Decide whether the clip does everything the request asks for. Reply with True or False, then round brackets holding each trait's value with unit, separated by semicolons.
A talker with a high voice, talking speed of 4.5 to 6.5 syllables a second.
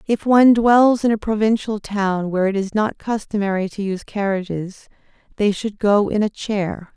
True (205 Hz; 5.0 syllables/s)